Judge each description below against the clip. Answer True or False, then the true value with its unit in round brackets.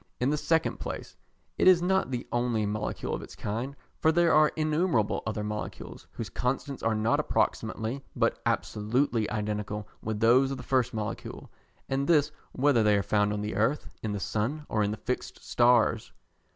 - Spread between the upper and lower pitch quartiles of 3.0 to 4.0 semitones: False (4.8 semitones)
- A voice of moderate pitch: False (120 Hz)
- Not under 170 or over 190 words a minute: True (180 wpm)